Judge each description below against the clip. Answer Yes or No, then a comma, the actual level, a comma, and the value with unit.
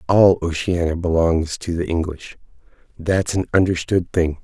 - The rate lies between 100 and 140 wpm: Yes, slow, 135 wpm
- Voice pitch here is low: Yes, very low, 85 Hz